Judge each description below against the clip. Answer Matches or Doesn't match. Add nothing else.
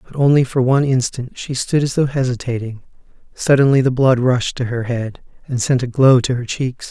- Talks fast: Matches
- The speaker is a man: Matches